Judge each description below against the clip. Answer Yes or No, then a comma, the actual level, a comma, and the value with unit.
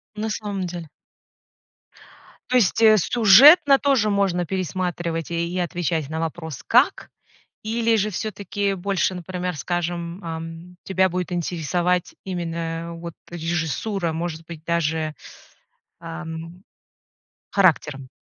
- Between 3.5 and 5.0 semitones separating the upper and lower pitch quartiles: No, average, 2.9 semitones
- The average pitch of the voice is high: No, medium, 175 Hz